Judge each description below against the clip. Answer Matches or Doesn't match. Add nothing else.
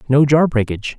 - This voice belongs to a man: Matches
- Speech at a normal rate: Matches